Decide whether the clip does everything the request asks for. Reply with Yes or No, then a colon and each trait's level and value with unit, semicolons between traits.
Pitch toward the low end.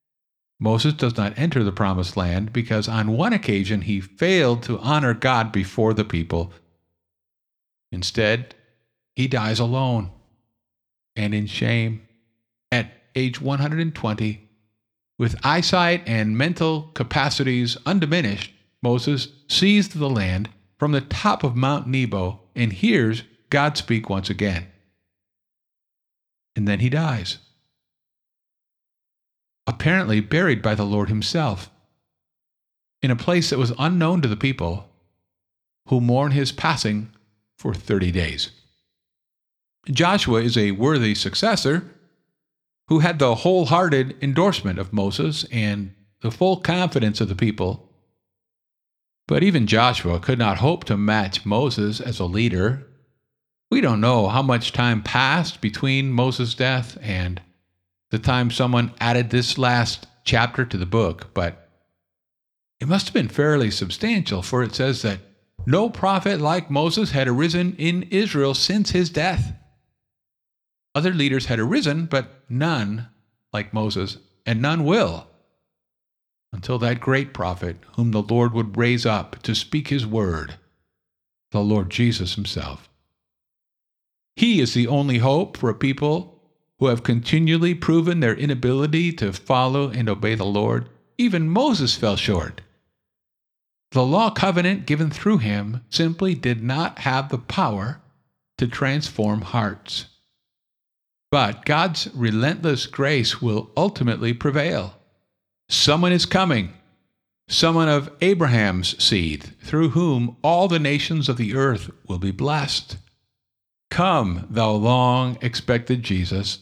Yes: low, 115 Hz